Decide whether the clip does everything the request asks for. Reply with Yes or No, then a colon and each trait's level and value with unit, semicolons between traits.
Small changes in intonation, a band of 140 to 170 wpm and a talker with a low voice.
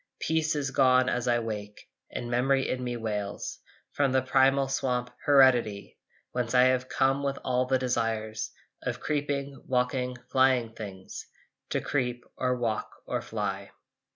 Yes: narrow, 2.0 semitones; average, 150 wpm; low, 125 Hz